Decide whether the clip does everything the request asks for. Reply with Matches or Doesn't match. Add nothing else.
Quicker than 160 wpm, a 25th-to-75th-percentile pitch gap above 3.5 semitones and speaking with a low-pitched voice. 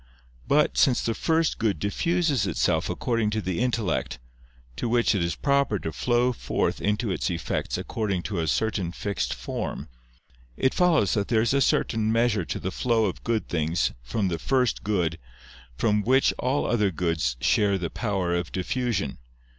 Matches